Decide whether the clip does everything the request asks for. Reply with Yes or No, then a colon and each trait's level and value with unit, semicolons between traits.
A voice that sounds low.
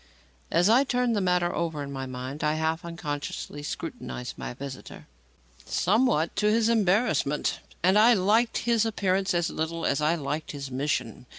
No: medium, 170 Hz